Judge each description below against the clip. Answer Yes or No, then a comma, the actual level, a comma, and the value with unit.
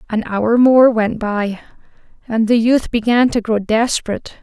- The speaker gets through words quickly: No, average, 165 wpm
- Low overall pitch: No, high, 225 Hz